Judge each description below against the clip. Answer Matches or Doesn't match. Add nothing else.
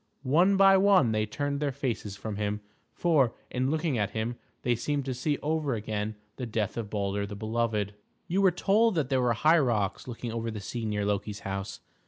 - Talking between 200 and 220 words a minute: Matches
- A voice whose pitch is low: Matches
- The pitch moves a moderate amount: Doesn't match